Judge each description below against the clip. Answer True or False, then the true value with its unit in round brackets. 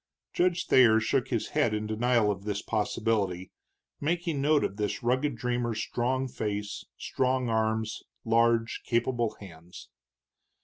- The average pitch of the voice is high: False (115 Hz)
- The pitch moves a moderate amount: True (3.2 semitones)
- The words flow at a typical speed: False (130 wpm)